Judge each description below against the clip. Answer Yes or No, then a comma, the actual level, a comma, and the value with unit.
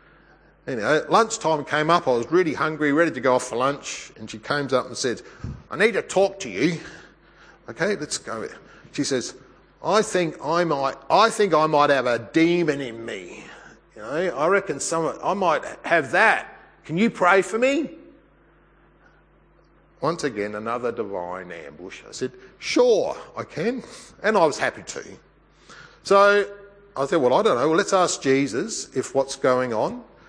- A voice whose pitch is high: No, medium, 160 Hz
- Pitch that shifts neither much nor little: No, wide, 6.8 semitones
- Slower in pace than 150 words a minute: No, average, 175 wpm